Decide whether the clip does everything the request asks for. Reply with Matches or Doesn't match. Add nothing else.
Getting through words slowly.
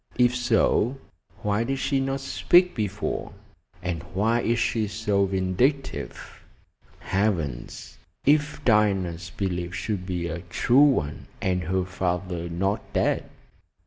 Matches